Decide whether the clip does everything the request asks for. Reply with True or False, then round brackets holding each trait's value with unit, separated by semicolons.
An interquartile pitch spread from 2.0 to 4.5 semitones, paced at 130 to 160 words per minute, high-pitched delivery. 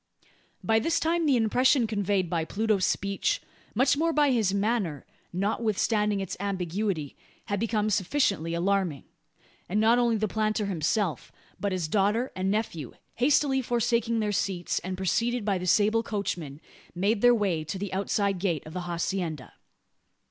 True (3.7 semitones; 155 wpm; 205 Hz)